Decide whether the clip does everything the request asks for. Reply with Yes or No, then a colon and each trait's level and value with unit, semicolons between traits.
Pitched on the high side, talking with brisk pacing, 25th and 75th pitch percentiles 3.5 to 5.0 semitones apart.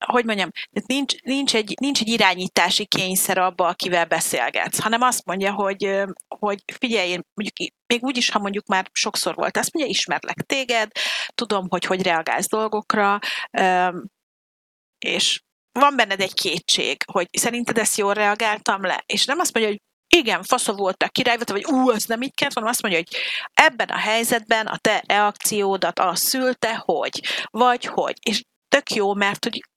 Yes: high, 215 Hz; fast, 165 wpm; average, 3.9 semitones